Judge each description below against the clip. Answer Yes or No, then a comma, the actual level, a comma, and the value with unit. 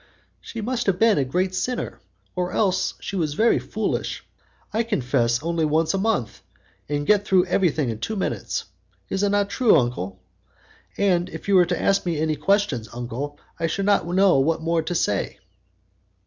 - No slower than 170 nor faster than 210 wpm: Yes, average, 180 wpm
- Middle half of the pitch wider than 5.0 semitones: Yes, wide, 5.5 semitones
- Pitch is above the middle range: No, medium, 175 Hz